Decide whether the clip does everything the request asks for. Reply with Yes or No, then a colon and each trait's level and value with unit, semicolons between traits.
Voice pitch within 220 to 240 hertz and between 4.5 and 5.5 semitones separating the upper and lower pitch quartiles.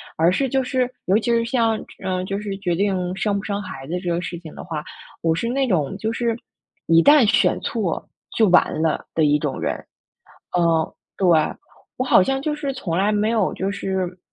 No: high, 195 Hz; average, 5.0 semitones